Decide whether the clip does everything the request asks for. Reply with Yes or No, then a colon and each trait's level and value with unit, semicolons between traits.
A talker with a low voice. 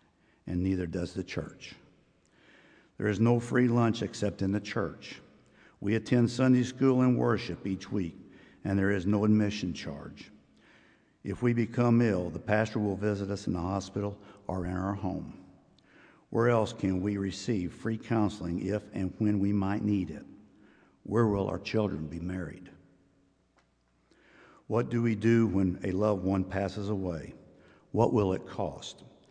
Yes: low, 100 Hz